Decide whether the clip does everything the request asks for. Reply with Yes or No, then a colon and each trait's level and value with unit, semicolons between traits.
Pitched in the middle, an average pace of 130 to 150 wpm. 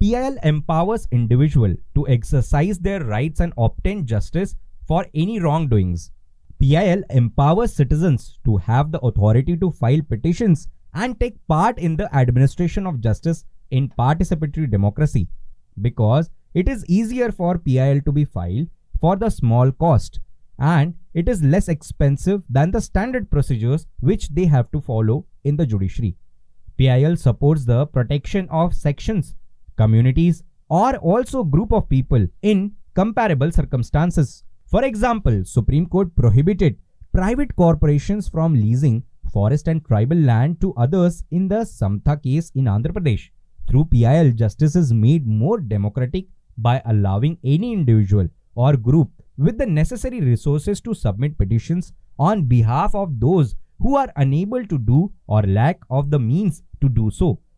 Yes: medium, 145 Hz; average, 145 wpm